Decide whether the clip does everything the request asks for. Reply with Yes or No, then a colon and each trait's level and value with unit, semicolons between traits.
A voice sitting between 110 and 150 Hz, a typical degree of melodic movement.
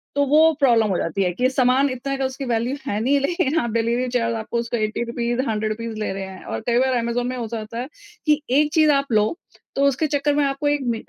No: high, 245 Hz; average, 3.5 semitones